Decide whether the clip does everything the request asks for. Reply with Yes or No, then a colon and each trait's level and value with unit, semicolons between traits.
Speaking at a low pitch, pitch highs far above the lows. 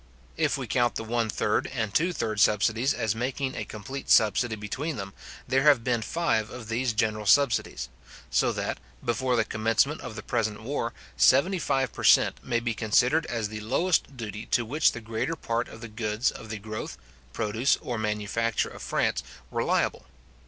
No: low, 115 Hz; average, 3.3 semitones